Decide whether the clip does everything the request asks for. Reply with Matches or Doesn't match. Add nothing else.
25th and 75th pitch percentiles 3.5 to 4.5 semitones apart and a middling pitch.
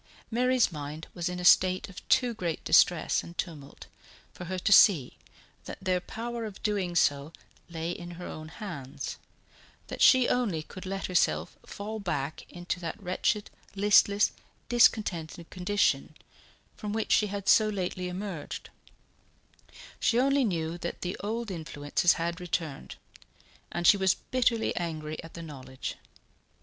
Matches